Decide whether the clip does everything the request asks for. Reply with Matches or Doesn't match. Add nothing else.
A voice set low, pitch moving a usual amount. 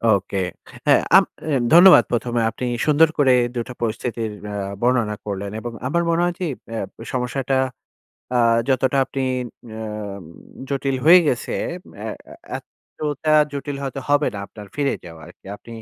Matches